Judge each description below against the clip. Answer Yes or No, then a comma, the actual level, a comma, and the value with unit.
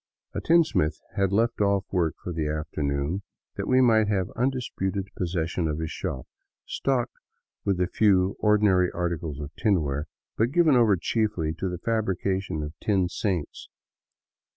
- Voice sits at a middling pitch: No, very low, 95 Hz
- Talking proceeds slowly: No, average, 150 wpm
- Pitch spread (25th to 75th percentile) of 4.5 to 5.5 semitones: Yes, average, 4.8 semitones